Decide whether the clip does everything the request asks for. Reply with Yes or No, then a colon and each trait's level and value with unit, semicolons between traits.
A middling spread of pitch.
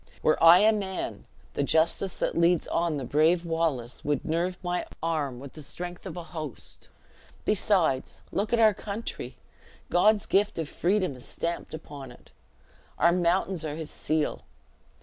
Yes: average, 3.3 semitones